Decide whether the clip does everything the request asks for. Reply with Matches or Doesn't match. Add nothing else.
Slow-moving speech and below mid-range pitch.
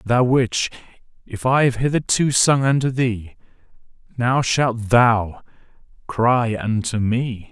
Matches